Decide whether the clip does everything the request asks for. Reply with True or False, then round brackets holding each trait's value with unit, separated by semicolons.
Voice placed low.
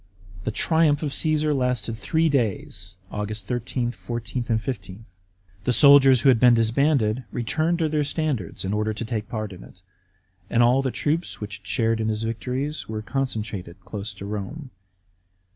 True (120 Hz)